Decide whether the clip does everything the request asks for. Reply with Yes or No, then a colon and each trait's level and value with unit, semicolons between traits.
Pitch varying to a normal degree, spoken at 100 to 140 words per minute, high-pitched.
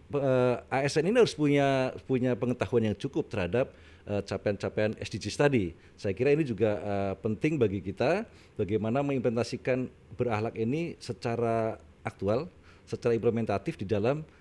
No: average, 4.1 semitones; slow, 135 wpm; low, 115 Hz